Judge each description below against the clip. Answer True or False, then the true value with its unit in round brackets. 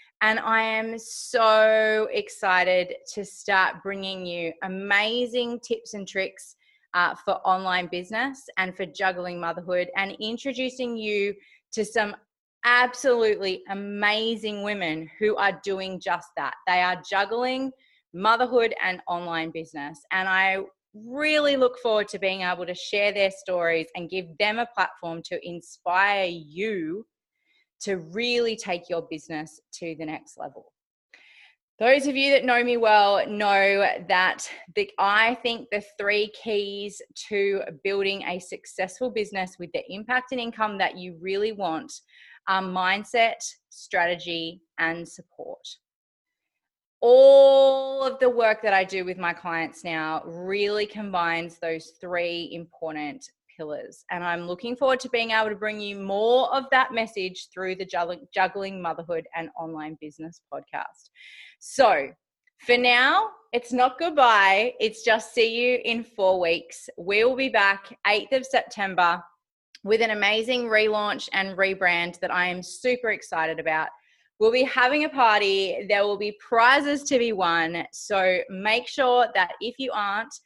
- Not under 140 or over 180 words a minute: True (145 wpm)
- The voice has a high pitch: True (205 Hz)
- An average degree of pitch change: True (4.9 semitones)